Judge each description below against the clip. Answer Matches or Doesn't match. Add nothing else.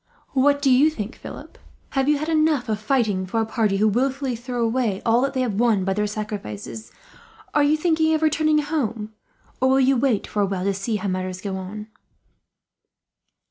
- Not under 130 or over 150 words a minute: Doesn't match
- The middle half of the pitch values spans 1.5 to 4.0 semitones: Doesn't match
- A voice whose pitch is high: Matches